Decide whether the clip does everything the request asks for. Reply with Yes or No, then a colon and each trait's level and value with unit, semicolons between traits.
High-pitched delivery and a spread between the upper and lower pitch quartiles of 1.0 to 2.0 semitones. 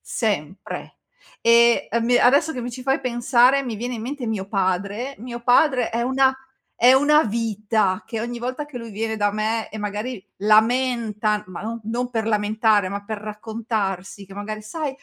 No: high, 225 Hz; average, 2.8 semitones